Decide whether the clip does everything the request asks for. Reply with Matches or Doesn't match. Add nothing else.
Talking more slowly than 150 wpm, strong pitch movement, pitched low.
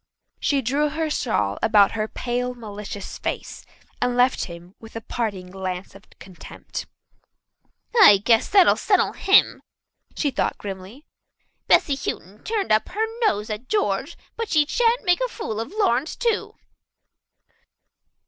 Doesn't match